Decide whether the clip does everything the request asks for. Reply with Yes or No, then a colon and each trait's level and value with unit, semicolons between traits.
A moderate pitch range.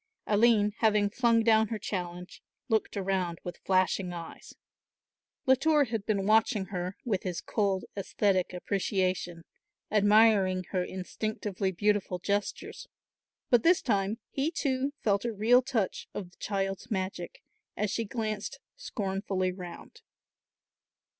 Yes: average, 3.0 semitones